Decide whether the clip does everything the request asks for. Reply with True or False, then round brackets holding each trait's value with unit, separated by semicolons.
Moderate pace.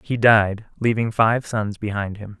True (175 wpm)